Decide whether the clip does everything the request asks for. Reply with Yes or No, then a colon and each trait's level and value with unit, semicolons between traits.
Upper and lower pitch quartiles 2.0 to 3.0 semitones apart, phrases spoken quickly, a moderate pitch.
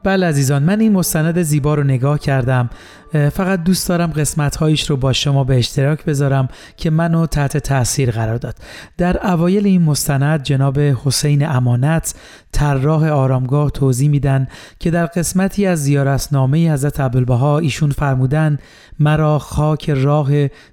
No: average, 2.7 semitones; average, 140 wpm; medium, 145 Hz